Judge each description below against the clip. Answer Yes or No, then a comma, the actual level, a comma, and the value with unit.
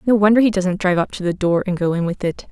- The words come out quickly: Yes, fast, 335 wpm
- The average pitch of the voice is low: No, high, 190 Hz